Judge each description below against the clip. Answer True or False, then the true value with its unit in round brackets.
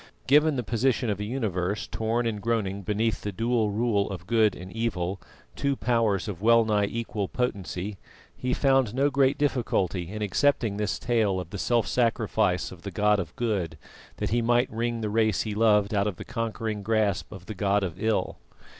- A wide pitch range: False (2.8 semitones)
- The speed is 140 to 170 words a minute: False (190 wpm)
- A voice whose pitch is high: False (110 Hz)